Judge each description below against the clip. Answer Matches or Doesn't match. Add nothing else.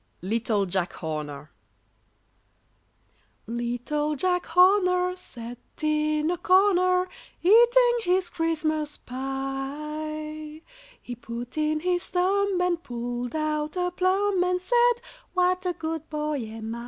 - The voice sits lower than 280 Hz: Doesn't match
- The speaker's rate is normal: Doesn't match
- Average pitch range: Doesn't match